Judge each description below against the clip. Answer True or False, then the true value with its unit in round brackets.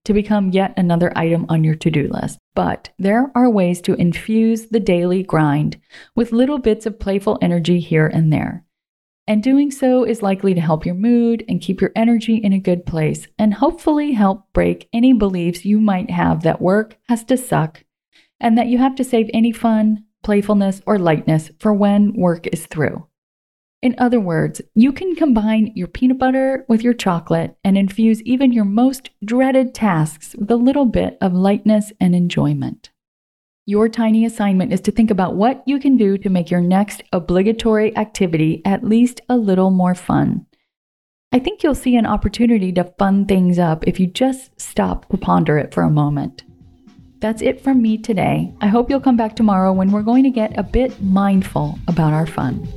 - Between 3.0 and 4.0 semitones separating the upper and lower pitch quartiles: False (4.5 semitones)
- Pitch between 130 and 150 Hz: False (210 Hz)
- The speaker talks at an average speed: True (190 wpm)